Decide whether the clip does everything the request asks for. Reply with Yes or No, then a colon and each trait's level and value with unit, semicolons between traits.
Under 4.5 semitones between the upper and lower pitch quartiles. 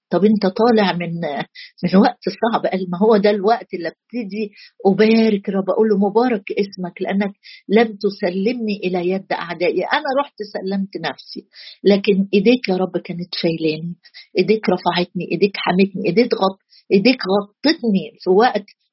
Yes: average, 2.9 semitones